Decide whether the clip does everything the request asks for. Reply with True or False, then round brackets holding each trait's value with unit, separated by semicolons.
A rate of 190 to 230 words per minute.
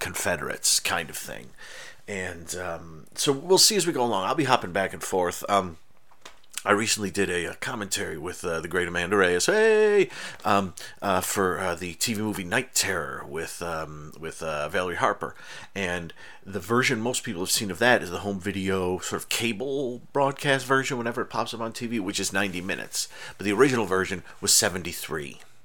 True (195 wpm)